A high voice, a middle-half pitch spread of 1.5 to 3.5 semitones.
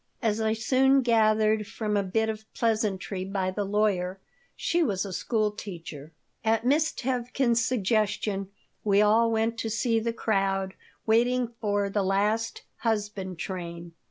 Yes: high, 215 Hz; narrow, 2.6 semitones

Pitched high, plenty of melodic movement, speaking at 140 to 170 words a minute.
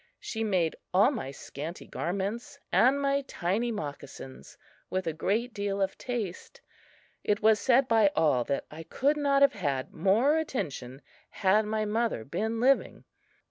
Yes: high, 210 Hz; wide, 6.3 semitones; average, 150 wpm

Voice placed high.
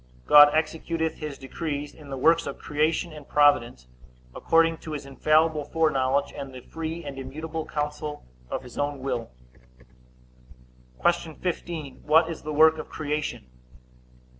No: medium, 150 Hz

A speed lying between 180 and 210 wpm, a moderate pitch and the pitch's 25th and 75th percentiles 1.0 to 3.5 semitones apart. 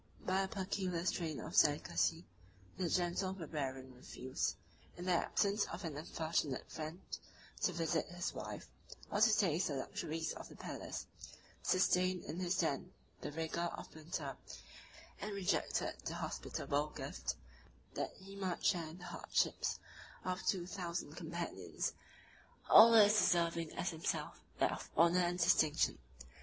No: average, 145 wpm; medium, 175 Hz; narrow, 2.6 semitones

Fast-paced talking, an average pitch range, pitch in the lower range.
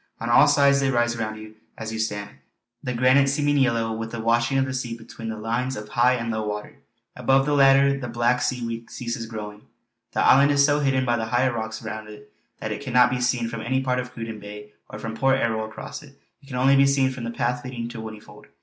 Yes: fast, 240 wpm; average, 3.0 semitones; low, 120 Hz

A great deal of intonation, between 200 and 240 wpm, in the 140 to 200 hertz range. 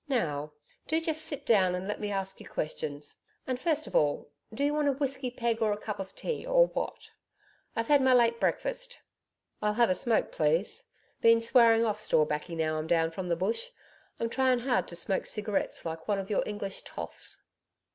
No: wide, 6.4 semitones; fast, 205 wpm; high, 220 Hz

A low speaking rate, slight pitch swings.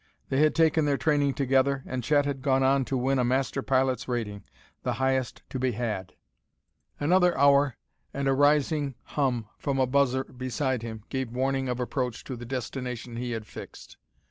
No: average, 180 wpm; narrow, 2.0 semitones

